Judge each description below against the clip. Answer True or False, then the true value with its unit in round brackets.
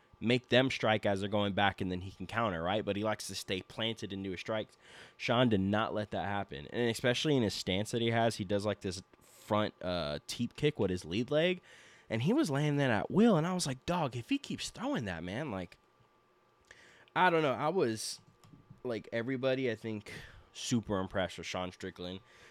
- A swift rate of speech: True (220 wpm)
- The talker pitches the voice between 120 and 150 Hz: False (110 Hz)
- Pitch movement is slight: False (4.1 semitones)